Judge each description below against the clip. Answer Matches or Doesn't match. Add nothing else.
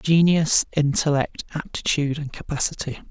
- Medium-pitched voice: Matches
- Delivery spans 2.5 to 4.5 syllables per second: Doesn't match